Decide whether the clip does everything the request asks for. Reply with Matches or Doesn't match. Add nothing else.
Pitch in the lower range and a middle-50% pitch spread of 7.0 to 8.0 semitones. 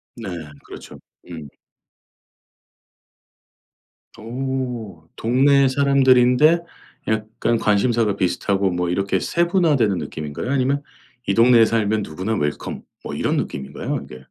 Doesn't match